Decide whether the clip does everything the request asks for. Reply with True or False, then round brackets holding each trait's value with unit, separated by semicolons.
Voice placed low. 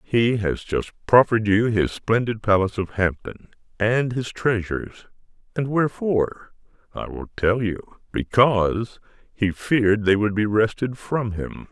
True (110 Hz)